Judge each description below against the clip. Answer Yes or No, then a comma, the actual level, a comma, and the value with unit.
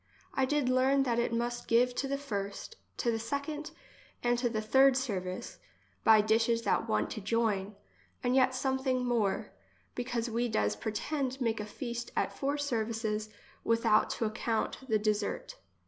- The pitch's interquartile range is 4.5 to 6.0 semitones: No, average, 3.1 semitones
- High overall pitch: Yes, high, 235 Hz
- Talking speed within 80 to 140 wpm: No, average, 165 wpm